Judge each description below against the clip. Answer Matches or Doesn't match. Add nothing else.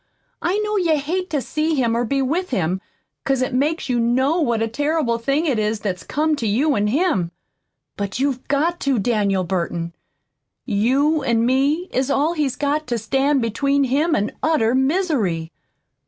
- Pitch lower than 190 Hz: Doesn't match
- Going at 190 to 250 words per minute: Doesn't match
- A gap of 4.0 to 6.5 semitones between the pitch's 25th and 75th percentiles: Matches